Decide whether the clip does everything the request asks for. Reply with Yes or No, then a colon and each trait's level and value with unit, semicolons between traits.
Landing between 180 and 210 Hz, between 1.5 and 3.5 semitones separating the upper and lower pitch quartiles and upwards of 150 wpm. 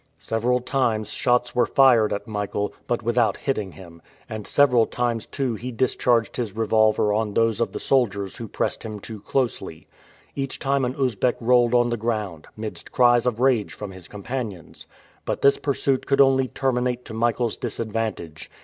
No: low, 115 Hz; average, 2.8 semitones; average, 170 wpm